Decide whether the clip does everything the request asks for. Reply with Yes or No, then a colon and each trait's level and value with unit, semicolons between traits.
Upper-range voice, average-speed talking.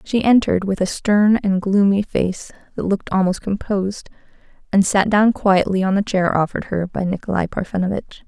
Yes: high, 195 Hz; average, 175 wpm